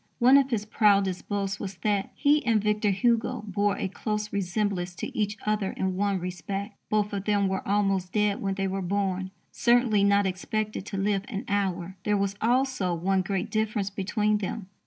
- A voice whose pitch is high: Yes, high, 200 Hz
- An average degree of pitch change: No, narrow, 1.8 semitones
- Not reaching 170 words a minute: No, average, 185 wpm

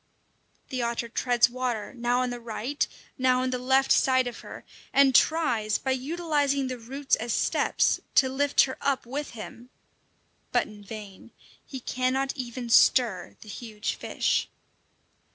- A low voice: No, very high, 255 Hz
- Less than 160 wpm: Yes, average, 150 wpm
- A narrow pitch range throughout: Yes, narrow, 2.3 semitones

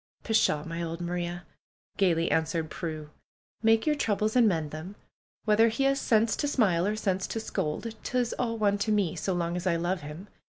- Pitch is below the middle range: No, high, 190 Hz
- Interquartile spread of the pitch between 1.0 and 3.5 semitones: No, average, 4.8 semitones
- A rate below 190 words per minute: No, average, 195 wpm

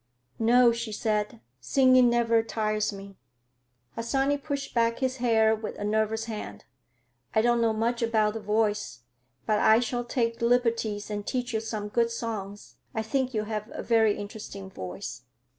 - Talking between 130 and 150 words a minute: No, average, 160 wpm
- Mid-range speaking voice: No, high, 225 Hz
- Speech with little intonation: Yes, narrow, 2.0 semitones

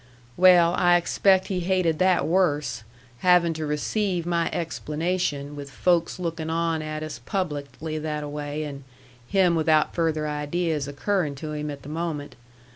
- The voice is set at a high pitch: No, medium, 160 Hz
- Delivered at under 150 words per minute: No, average, 155 wpm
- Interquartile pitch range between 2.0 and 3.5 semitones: Yes, average, 2.9 semitones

